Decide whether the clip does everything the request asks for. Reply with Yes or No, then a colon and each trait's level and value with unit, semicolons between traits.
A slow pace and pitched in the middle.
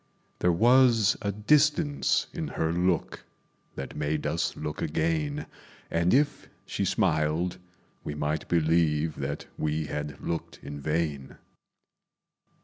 No: slow, 120 wpm; very low, 85 Hz